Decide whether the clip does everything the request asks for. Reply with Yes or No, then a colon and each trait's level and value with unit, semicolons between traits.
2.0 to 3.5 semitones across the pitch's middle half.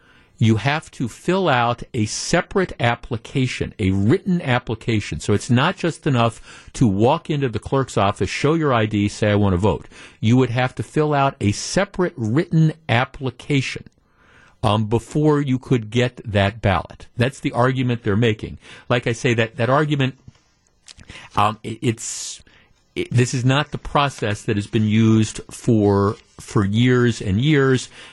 No: average, 4.2 semitones